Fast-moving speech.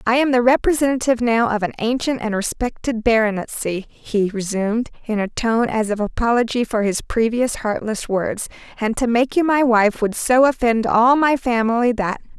No: average, 180 wpm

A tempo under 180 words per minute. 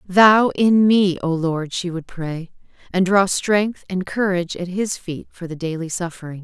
No: average, 185 wpm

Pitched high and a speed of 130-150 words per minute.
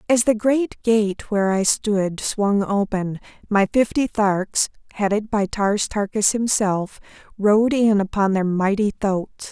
Yes: high, 205 Hz; average, 145 wpm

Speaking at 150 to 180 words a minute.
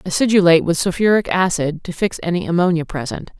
Yes: average, 160 wpm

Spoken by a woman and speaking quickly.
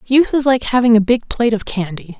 Yes: female; fast, 245 wpm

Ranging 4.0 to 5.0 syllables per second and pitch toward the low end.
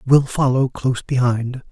Yes: 4.6 syllables/s; low, 130 Hz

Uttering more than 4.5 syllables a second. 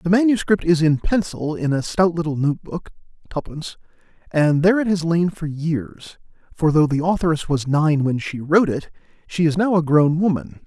Yes: 5.1 syllables/s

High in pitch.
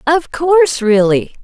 Yes: very high, 275 Hz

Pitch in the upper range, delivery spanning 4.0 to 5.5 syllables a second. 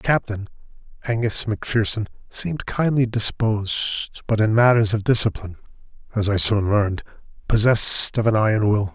No: low, 110 Hz; 5.3 syllables/s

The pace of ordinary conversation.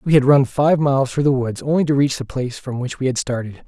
No: fast, 295 wpm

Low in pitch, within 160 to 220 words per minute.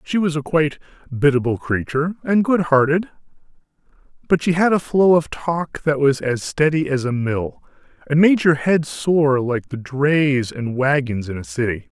No: medium, 145 Hz; average, 180 wpm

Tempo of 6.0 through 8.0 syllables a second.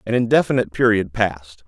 Yes: 6.5 syllables/s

